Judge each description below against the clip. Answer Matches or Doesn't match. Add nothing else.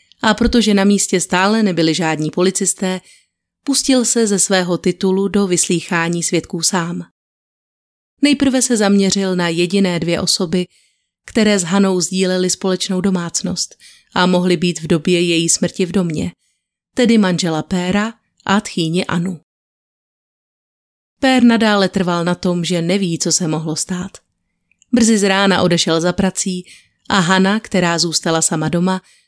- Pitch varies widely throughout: Doesn't match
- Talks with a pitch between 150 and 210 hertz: Matches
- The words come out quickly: Doesn't match